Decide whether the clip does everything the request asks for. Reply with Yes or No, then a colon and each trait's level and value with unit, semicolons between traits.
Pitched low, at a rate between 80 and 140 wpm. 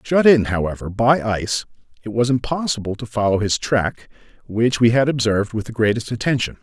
No: low, 115 Hz; average, 180 wpm